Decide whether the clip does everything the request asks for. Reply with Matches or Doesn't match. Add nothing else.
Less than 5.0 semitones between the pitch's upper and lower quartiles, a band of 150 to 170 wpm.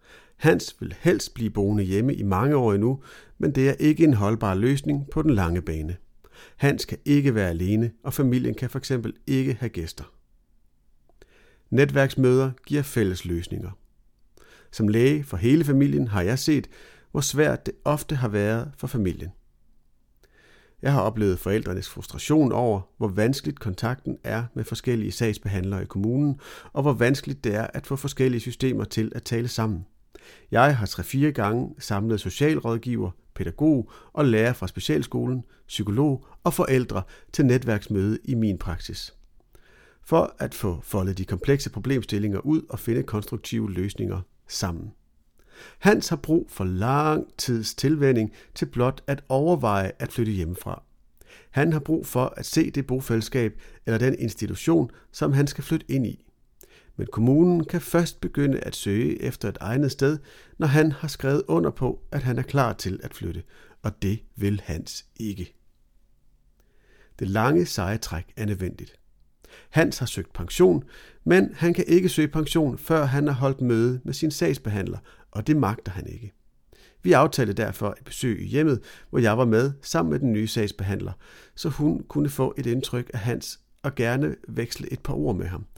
Doesn't match